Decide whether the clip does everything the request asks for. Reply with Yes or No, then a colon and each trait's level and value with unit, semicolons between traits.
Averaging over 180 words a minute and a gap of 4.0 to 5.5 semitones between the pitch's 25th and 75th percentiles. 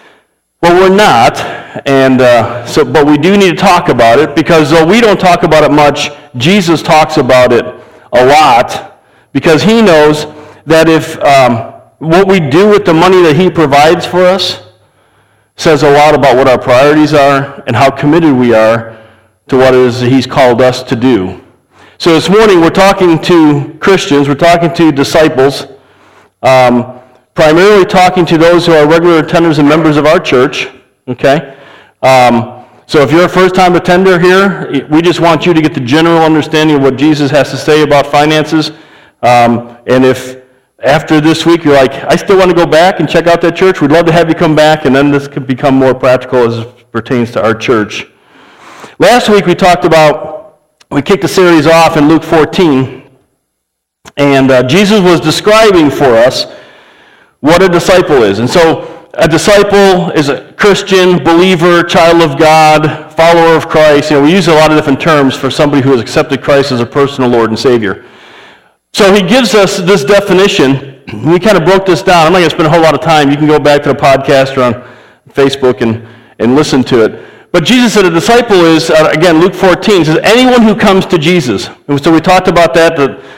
Yes: average, 200 wpm; average, 4.4 semitones